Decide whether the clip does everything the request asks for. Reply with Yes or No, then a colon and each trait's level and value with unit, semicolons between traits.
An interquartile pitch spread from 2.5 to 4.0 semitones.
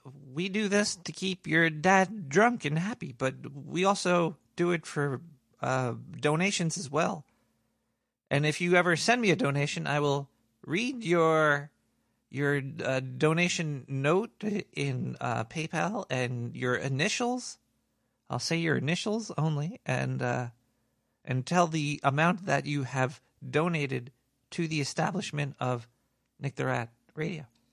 No: average, 4.9 semitones